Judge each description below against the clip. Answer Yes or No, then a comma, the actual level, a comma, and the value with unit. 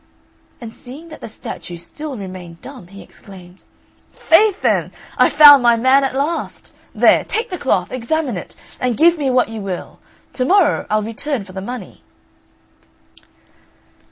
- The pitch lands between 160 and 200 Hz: No, very high, 250 Hz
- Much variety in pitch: Yes, wide, 7.0 semitones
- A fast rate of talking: No, average, 155 wpm